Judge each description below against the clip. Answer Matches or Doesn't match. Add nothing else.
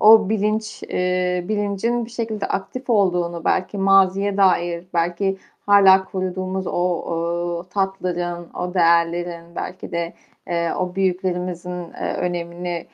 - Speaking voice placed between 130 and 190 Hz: Matches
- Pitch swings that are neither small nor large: Doesn't match